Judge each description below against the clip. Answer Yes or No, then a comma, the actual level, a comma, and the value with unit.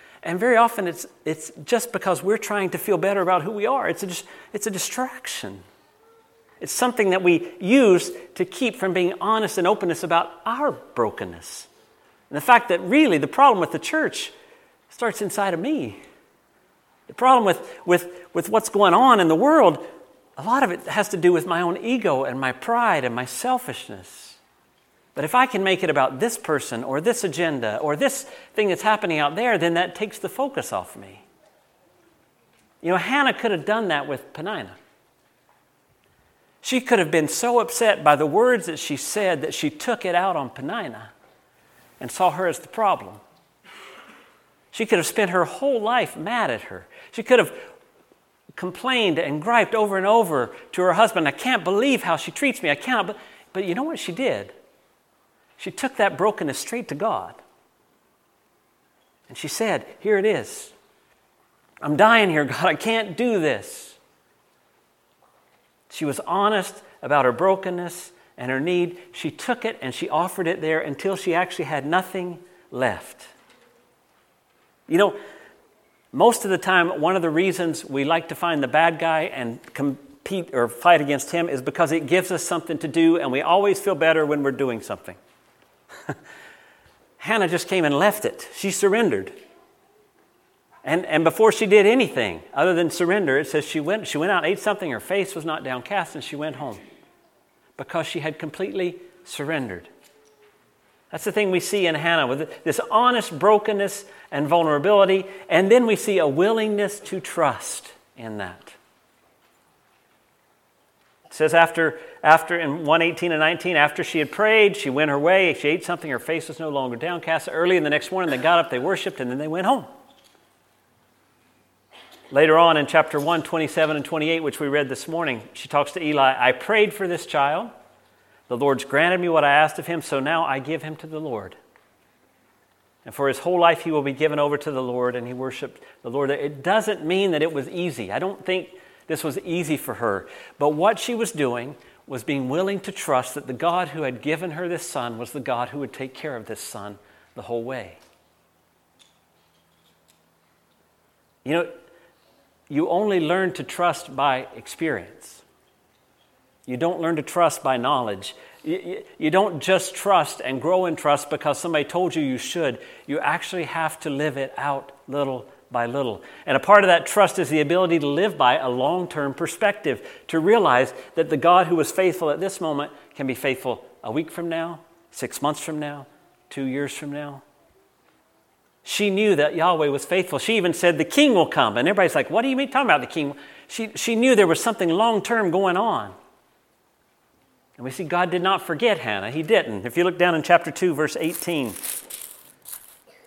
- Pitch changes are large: Yes, wide, 5.8 semitones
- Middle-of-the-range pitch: Yes, medium, 175 Hz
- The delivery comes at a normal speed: Yes, average, 185 wpm